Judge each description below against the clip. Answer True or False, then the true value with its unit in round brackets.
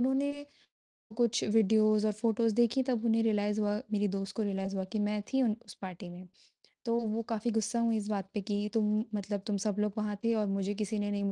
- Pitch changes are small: True (1.9 semitones)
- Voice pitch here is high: True (210 Hz)